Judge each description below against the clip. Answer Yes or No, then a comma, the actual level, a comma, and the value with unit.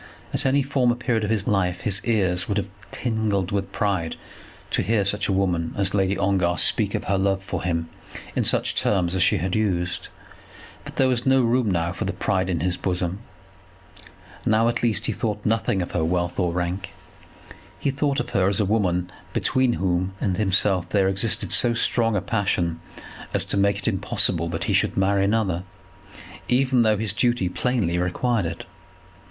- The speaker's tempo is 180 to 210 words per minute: Yes, average, 185 wpm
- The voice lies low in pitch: Yes, low, 100 Hz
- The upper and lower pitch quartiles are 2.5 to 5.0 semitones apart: Yes, average, 3.7 semitones